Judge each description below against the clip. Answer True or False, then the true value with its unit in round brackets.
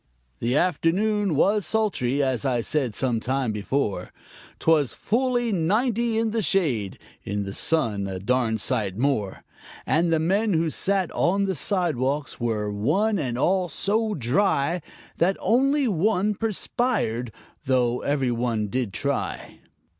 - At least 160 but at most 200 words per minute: False (140 wpm)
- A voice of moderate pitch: True (150 Hz)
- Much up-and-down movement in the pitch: True (8.9 semitones)